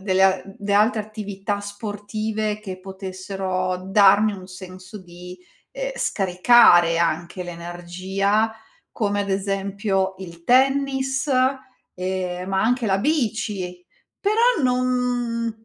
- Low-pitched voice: No, high, 200 Hz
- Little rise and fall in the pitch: No, average, 3.1 semitones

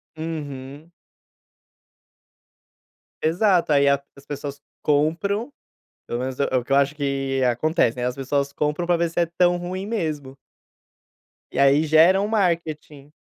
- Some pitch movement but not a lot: Yes, average, 3.6 semitones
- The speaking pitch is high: No, medium, 150 Hz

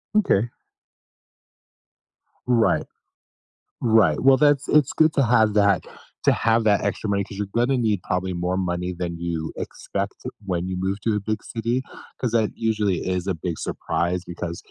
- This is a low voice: Yes, low, 100 Hz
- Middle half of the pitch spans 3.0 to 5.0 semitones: Yes, average, 4.2 semitones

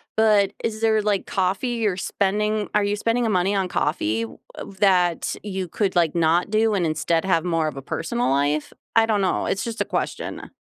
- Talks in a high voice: Yes, high, 195 Hz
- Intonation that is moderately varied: Yes, average, 3.9 semitones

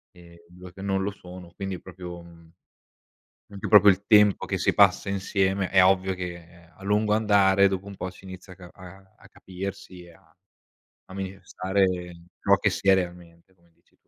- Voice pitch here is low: Yes, very low, 95 Hz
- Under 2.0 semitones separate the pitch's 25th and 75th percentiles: Yes, narrow, 1.6 semitones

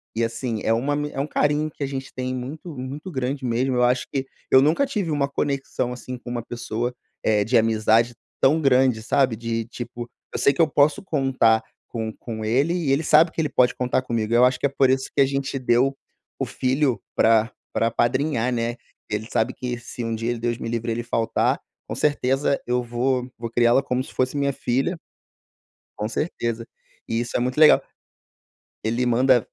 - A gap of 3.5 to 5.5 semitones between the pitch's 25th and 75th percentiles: No, average, 2.9 semitones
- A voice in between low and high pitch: No, low, 125 Hz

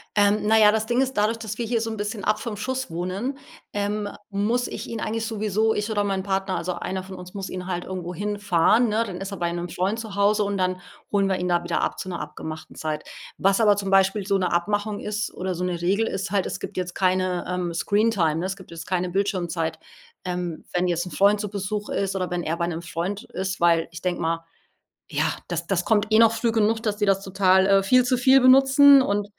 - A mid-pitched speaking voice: No, high, 195 Hz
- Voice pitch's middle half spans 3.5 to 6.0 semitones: No, average, 2.9 semitones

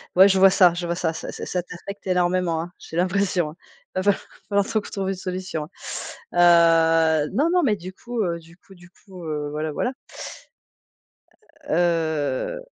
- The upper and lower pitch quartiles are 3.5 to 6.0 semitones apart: No, average, 2.8 semitones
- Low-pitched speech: No, medium, 175 Hz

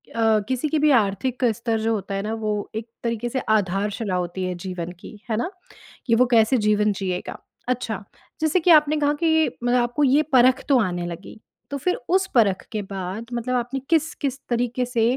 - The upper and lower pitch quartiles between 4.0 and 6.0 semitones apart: Yes, average, 4.3 semitones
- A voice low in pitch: No, high, 230 Hz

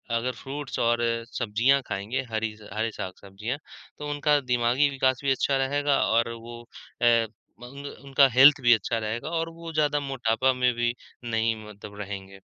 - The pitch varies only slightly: No, average, 3.7 semitones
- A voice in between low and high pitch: No, low, 125 Hz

